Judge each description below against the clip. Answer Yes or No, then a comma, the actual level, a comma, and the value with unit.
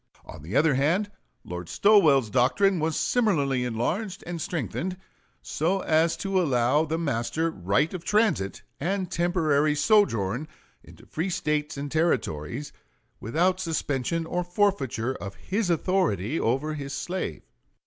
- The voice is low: No, medium, 155 Hz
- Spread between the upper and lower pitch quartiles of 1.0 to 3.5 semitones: No, wide, 5.6 semitones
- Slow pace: Yes, slow, 130 wpm